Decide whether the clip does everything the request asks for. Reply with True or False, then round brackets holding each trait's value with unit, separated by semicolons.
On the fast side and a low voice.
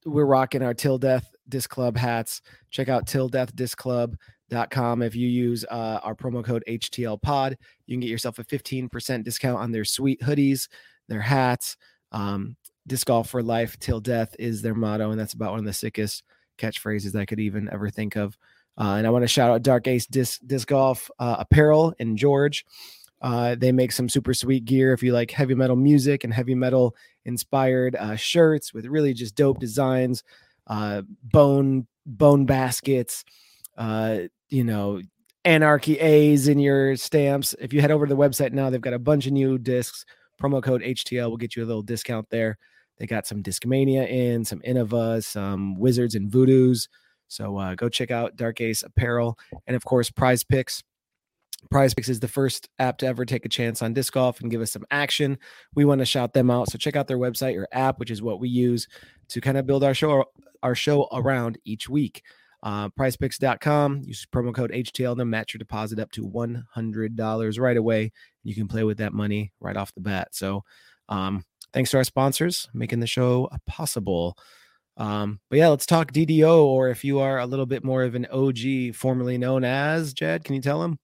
False (195 wpm; 125 Hz)